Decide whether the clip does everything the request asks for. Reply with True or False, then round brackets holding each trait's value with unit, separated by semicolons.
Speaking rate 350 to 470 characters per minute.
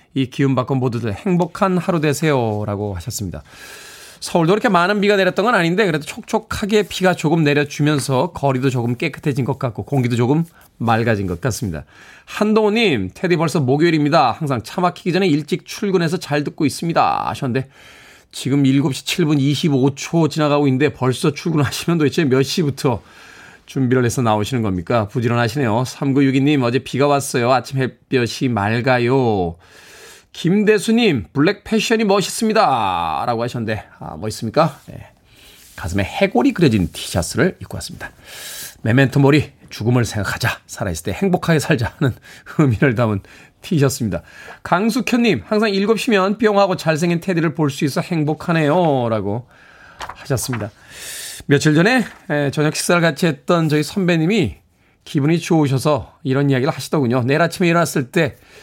True (355 characters per minute)